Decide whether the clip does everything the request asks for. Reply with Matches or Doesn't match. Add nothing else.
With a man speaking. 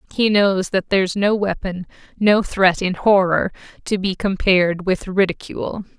Doesn't match